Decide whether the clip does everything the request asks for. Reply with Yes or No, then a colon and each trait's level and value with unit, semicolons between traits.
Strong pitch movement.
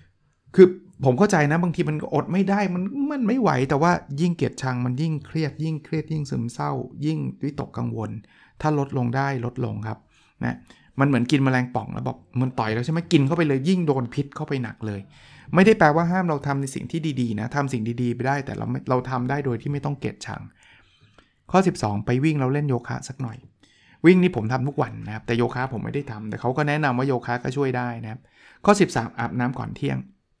No: average, 4.2 semitones